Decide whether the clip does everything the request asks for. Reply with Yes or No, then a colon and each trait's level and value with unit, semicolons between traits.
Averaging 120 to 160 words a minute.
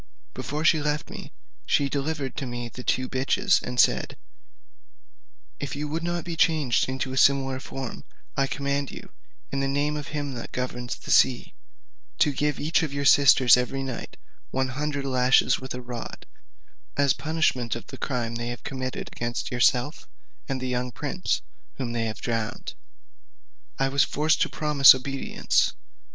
No: average, 170 wpm